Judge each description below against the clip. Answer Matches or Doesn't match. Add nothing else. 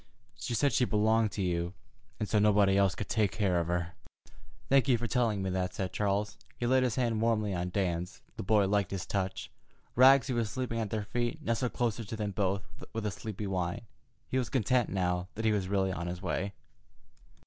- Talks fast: Matches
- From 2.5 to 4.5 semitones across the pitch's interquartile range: Matches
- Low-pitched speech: Matches